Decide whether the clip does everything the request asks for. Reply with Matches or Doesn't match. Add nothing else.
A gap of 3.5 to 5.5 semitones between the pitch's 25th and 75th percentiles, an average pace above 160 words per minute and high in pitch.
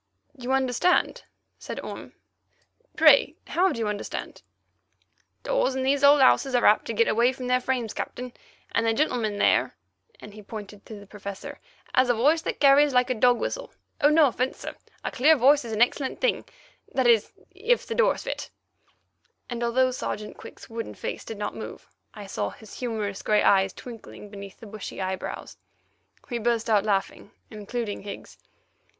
Matches